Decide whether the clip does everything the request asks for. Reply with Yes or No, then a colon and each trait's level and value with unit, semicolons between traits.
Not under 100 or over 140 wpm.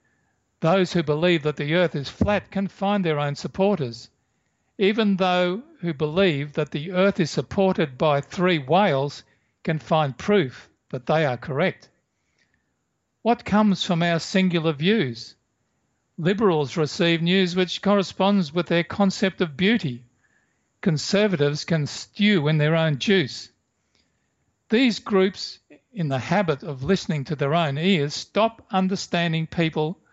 Yes: slow, 135 wpm